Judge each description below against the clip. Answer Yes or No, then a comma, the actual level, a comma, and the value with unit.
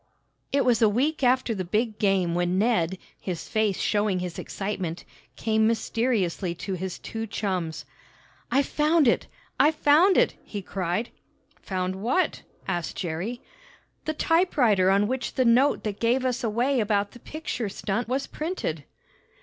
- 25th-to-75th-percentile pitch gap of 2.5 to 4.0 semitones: No, average, 5.2 semitones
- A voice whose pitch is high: Yes, high, 220 Hz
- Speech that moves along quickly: No, average, 150 wpm